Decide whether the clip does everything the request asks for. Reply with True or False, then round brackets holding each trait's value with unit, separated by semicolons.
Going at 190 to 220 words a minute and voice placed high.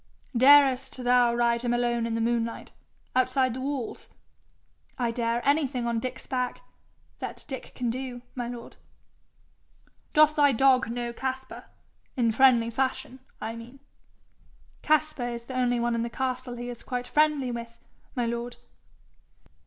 False (145 wpm; 245 Hz)